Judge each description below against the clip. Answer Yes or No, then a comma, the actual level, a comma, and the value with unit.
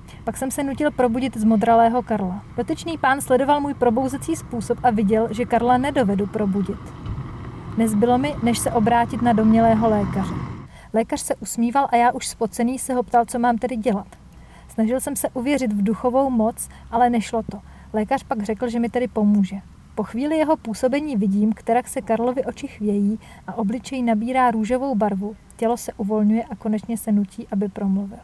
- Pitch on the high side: Yes, high, 235 Hz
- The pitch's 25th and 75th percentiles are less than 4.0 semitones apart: Yes, average, 2.8 semitones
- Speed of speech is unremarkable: No, fast, 175 wpm